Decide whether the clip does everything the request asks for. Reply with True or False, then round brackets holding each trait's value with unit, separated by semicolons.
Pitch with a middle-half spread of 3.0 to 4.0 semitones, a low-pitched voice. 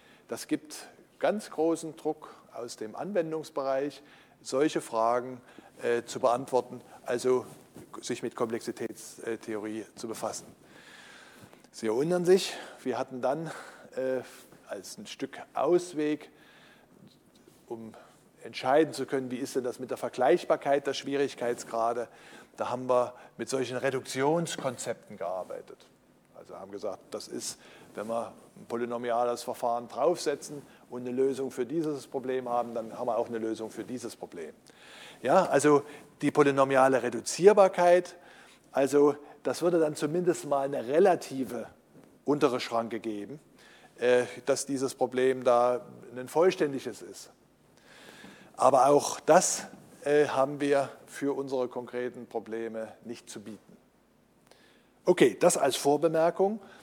True (3.4 semitones; 130 Hz)